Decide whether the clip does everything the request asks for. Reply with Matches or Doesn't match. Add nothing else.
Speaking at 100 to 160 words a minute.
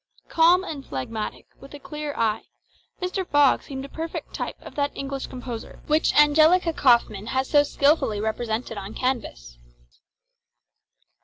Matches